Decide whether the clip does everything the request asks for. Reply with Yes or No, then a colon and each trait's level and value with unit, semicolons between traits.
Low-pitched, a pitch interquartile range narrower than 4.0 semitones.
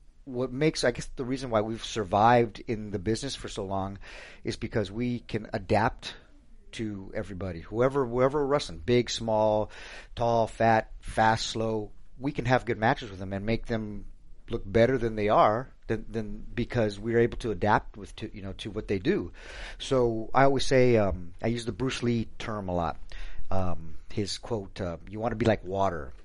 Yes: low, 110 Hz; average, 3.4 semitones